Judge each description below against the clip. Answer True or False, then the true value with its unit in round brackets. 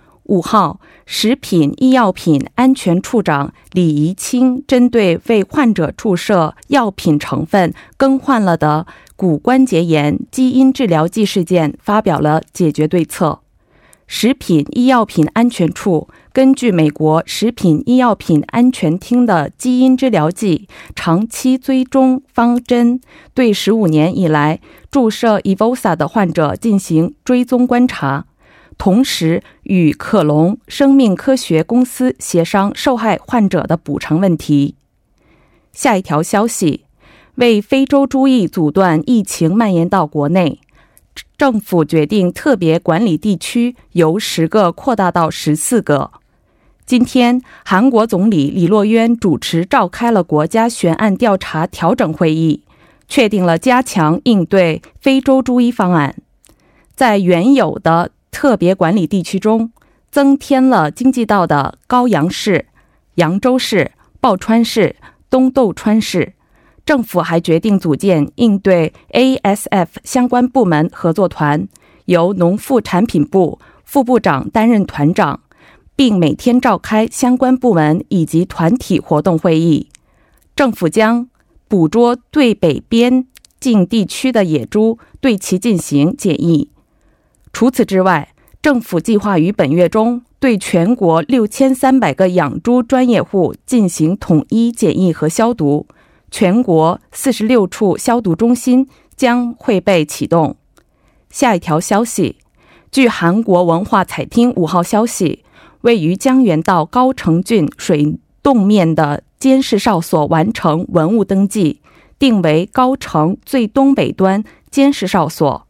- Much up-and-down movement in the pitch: True (6.7 semitones)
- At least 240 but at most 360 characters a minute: False (205 characters per minute)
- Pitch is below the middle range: False (200 Hz)